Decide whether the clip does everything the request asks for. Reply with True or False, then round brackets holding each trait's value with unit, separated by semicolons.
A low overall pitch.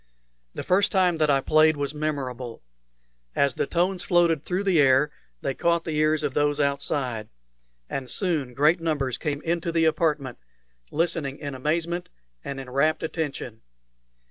False (150 Hz)